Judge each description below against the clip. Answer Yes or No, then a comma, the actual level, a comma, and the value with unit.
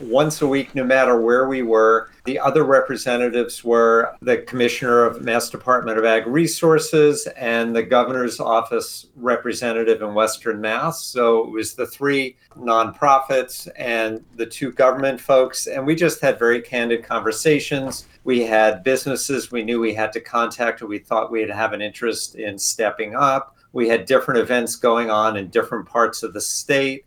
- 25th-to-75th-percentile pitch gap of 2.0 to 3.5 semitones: Yes, average, 3.0 semitones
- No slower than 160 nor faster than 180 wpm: Yes, average, 170 wpm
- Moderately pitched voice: No, low, 120 Hz